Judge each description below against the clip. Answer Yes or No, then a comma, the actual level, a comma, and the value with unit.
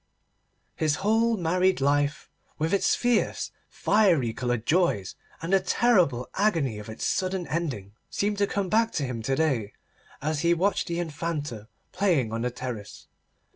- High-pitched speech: No, medium, 160 Hz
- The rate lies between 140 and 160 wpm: Yes, average, 155 wpm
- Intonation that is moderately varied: No, wide, 7.2 semitones